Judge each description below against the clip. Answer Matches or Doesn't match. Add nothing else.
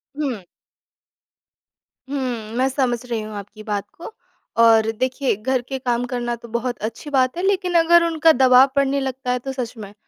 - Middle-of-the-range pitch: Doesn't match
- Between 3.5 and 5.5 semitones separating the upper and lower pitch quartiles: Doesn't match